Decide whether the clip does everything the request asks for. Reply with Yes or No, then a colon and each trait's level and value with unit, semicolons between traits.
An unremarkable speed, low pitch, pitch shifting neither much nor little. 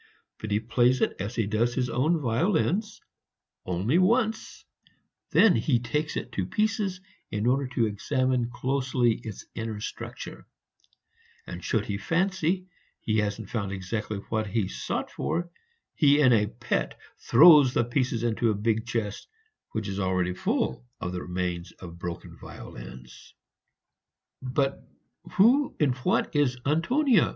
No: average, 145 wpm; low, 120 Hz; wide, 6.2 semitones